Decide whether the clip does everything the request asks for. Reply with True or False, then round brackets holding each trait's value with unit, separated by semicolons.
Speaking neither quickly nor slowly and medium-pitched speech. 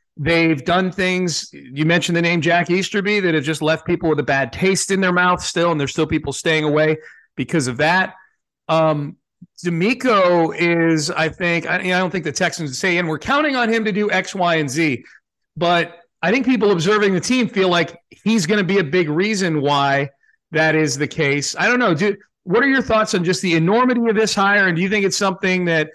False (225 wpm; 175 Hz)